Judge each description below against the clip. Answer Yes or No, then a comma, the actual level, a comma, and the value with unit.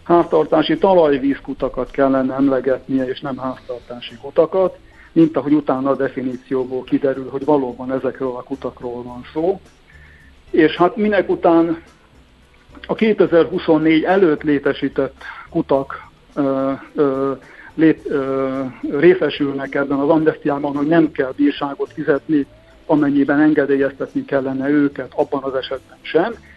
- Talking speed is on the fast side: No, average, 115 wpm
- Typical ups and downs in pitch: Yes, average, 3.1 semitones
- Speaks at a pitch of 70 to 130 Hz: No, medium, 140 Hz